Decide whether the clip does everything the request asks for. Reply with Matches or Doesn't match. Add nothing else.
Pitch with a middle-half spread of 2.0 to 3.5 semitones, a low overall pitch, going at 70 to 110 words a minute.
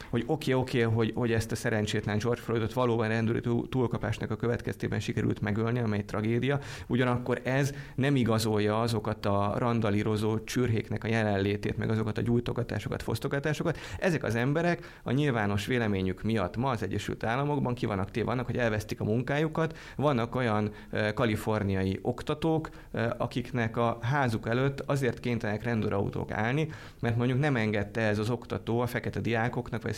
Doesn't match